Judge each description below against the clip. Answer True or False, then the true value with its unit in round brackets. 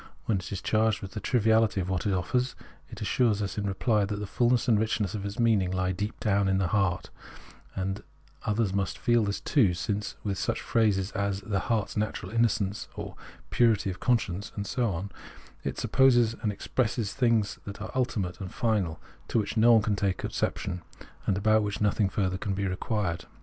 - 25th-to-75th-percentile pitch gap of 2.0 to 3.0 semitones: True (2.7 semitones)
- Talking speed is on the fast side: True (210 wpm)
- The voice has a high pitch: False (105 Hz)